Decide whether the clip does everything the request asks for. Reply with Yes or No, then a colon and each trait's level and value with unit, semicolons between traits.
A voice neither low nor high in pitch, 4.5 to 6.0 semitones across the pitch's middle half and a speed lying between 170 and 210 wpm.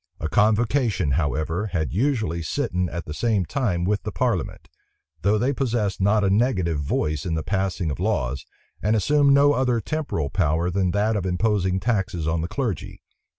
No: very low, 95 Hz; average, 5.1 semitones; average, 175 wpm